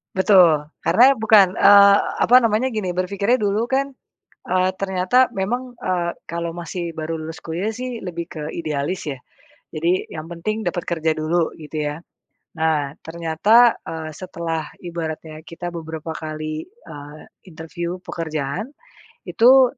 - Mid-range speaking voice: Yes, medium, 170 Hz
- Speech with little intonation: No, average, 4.1 semitones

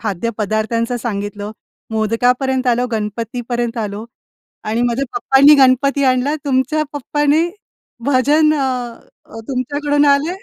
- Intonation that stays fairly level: No, average, 3.5 semitones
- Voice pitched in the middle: No, very high, 250 Hz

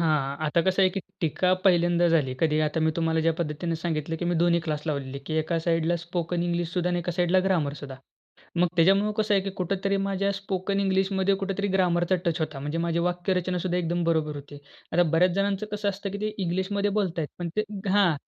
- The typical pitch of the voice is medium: Yes, medium, 175 Hz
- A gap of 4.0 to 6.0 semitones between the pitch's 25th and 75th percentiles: No, average, 2.9 semitones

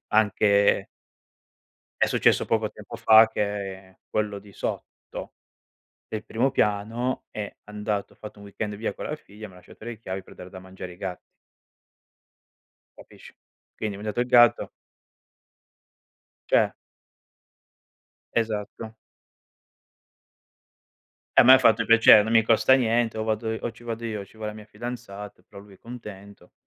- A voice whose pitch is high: No, low, 105 Hz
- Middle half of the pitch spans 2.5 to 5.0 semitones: No, narrow, 2.1 semitones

